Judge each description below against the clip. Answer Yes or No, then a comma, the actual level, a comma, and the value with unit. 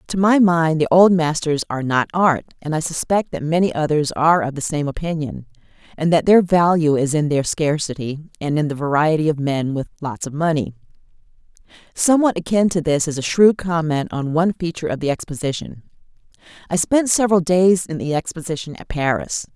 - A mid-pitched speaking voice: Yes, medium, 160 Hz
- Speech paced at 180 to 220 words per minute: Yes, average, 185 wpm